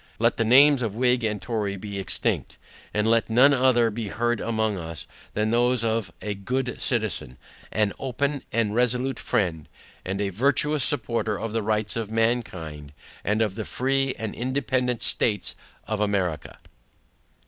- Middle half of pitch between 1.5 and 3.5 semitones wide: Yes, average, 3.2 semitones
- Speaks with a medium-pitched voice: No, low, 115 Hz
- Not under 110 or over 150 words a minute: No, average, 160 wpm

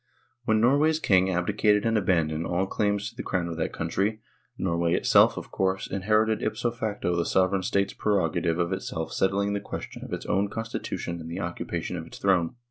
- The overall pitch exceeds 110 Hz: No, very low, 95 Hz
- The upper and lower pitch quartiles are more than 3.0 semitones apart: Yes, average, 3.4 semitones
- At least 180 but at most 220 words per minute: Yes, average, 195 wpm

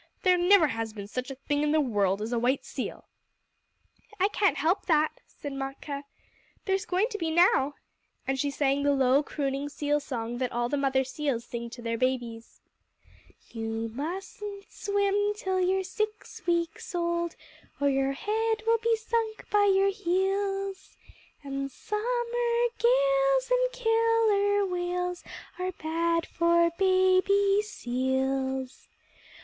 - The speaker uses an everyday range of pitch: No, wide, 6.8 semitones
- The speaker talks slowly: No, average, 145 wpm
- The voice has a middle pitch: No, very high, 335 Hz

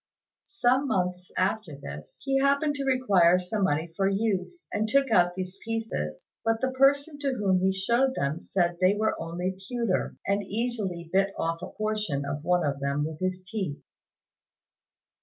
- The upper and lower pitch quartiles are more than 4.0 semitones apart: Yes, average, 5.1 semitones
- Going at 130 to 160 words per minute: No, average, 170 wpm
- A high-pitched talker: Yes, high, 195 Hz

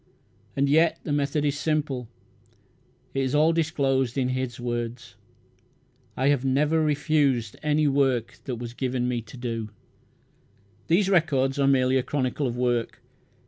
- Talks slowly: No, average, 145 wpm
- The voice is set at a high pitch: No, low, 135 Hz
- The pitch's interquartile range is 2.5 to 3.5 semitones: Yes, average, 3.1 semitones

